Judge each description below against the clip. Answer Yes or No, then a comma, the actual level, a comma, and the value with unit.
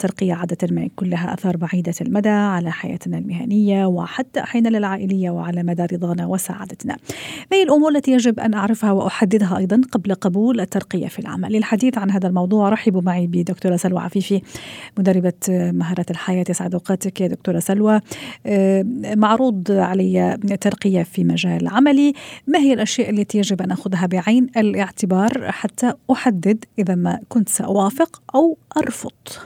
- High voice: Yes, high, 195 Hz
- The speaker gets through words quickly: Yes, fast, 145 wpm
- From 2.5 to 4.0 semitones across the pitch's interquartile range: Yes, average, 3.4 semitones